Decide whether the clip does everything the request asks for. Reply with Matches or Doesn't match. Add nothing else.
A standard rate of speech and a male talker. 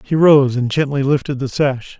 Doesn't match